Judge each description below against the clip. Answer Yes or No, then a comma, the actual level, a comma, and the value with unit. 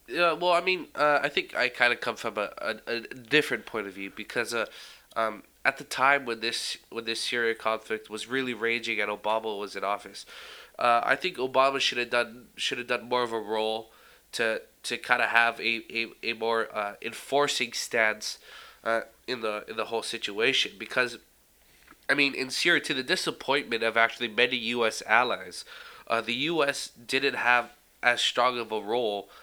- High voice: No, low, 120 Hz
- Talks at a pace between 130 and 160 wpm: No, average, 195 wpm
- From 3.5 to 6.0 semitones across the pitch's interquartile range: No, average, 3.0 semitones